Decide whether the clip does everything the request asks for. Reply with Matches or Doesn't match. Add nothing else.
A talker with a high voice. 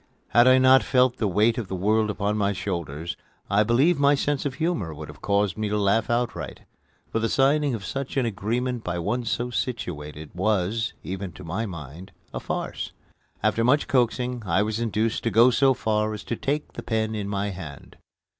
Doesn't match